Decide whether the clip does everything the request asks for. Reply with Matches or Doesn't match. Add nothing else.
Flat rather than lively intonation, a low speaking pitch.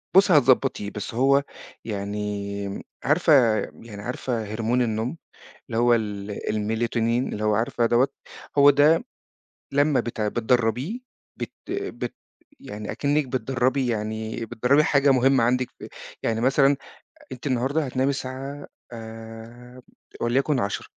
Doesn't match